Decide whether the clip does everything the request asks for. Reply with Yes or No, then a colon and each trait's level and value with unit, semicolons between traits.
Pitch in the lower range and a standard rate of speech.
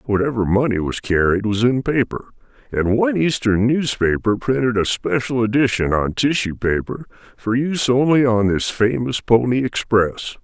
Yes: low, 115 Hz; average, 150 wpm